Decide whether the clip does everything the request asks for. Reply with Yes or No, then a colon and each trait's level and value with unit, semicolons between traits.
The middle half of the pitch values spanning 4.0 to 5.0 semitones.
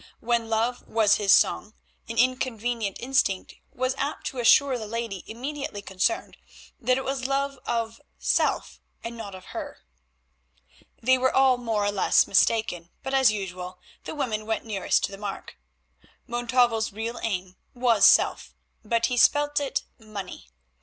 No: average, 3.6 semitones